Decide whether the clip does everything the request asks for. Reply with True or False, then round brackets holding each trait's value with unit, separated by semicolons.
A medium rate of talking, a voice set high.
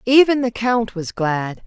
True (180 wpm; 225 Hz)